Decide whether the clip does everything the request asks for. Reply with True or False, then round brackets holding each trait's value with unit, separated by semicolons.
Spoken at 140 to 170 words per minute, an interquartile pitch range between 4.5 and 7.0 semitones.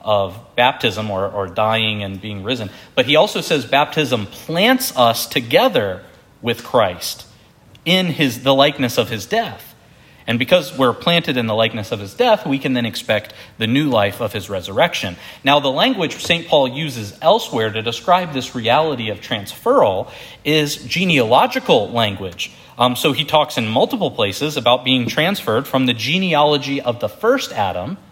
True (165 wpm; 5.3 semitones)